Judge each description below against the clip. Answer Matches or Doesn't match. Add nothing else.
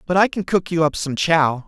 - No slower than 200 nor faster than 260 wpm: Doesn't match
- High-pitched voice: Doesn't match